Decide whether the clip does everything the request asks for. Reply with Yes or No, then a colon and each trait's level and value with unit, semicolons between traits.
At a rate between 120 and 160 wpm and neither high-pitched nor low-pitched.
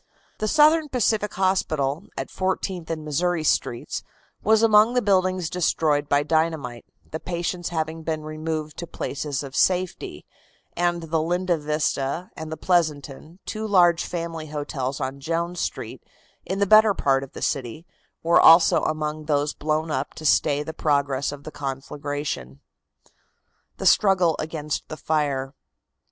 Yes: average, 145 wpm; medium, 160 Hz